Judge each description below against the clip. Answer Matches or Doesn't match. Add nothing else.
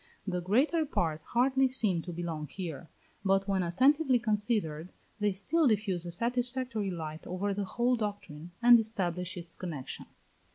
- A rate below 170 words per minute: Matches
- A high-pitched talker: Matches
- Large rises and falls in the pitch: Matches